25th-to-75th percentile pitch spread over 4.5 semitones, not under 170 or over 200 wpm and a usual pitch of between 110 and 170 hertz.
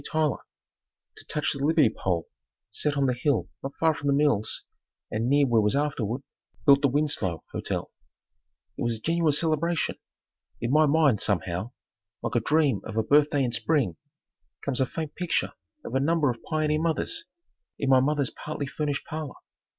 No: average, 4.0 semitones; average, 175 wpm; medium, 140 Hz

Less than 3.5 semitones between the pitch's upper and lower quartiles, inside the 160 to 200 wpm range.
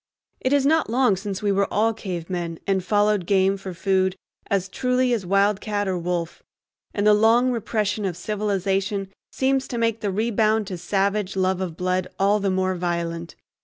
Yes: narrow, 2.4 semitones; average, 175 wpm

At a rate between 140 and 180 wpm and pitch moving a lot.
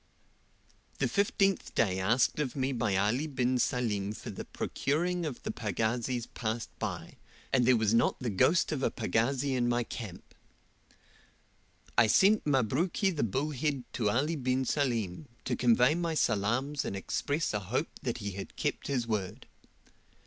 No: average, 155 wpm; average, 4.6 semitones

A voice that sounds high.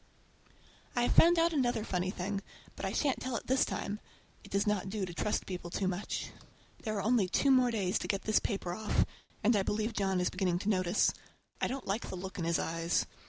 Yes: high, 200 Hz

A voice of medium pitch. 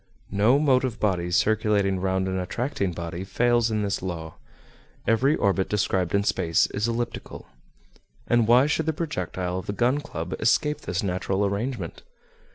No: low, 100 Hz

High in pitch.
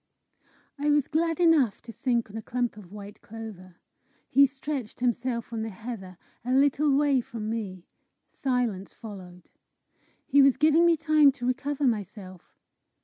Yes: high, 245 Hz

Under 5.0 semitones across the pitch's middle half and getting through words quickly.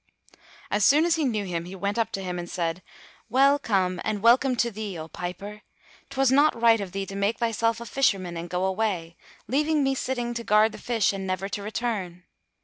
Yes: average, 4.4 semitones; fast, 215 wpm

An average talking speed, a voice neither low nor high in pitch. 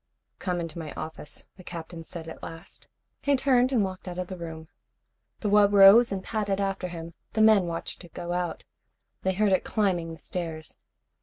Yes: average, 190 wpm; medium, 180 Hz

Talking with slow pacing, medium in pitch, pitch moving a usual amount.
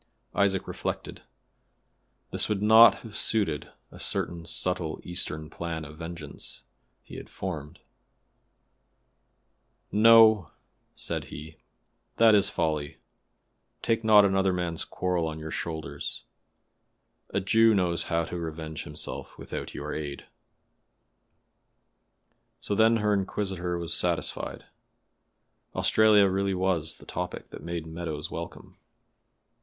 No: slow, 115 wpm; very low, 90 Hz; average, 4.0 semitones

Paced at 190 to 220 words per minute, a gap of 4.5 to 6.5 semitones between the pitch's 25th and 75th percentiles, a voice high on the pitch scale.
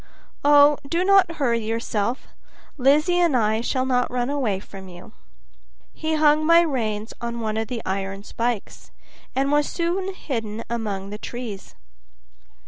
No: average, 145 wpm; wide, 5.5 semitones; high, 245 Hz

